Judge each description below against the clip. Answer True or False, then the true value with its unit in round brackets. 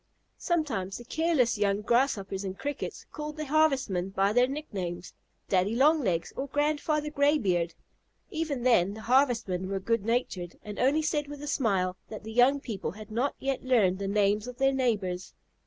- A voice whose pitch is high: True (235 Hz)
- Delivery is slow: False (170 wpm)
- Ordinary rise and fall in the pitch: False (6.5 semitones)